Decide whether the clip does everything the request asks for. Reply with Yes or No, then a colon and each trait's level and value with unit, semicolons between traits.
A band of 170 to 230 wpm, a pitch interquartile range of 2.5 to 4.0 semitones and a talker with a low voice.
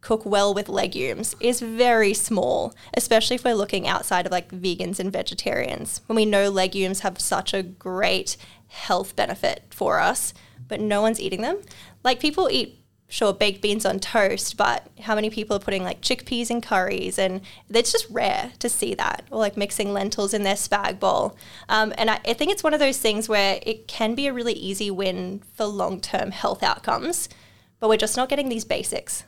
No: average, 200 wpm; average, 3.5 semitones; high, 215 Hz